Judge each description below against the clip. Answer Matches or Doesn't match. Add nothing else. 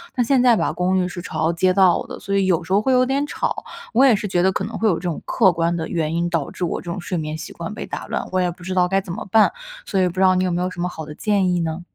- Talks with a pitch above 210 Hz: Doesn't match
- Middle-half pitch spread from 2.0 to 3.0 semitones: Matches